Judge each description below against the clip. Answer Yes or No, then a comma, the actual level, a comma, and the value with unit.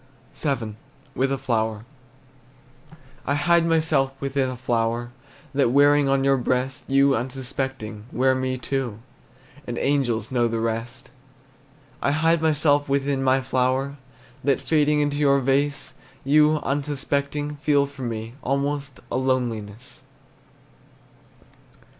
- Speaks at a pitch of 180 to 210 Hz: No, low, 135 Hz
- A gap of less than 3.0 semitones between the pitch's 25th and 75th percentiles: Yes, narrow, 2.4 semitones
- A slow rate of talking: Yes, slow, 120 wpm